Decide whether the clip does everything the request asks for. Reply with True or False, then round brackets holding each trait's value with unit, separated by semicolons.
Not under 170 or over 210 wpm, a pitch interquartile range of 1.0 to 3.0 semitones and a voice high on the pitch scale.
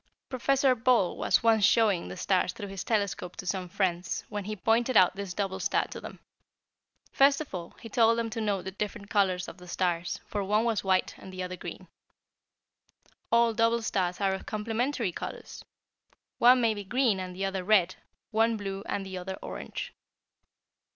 False (185 wpm; 3.5 semitones; 200 Hz)